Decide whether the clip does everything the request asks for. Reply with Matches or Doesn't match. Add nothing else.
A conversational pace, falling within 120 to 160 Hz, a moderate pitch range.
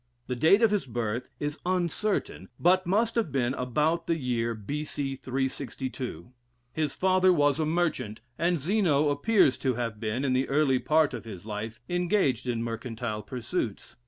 Doesn't match